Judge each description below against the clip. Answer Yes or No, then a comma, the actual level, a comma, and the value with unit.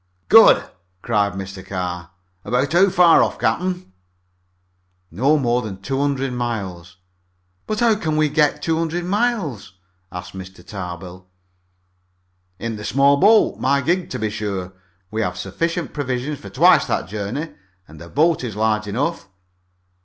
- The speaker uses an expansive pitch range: Yes, wide, 8.2 semitones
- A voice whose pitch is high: No, low, 120 Hz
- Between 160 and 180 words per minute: No, average, 145 wpm